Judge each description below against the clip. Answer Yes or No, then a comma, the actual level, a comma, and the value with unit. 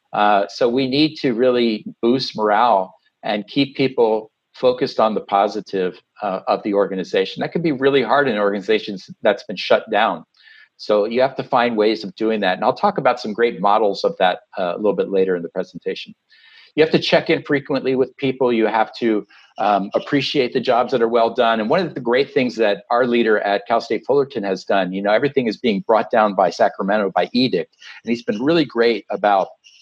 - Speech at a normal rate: No, fast, 215 wpm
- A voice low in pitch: Yes, low, 115 Hz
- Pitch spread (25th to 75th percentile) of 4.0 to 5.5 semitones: Yes, average, 4.5 semitones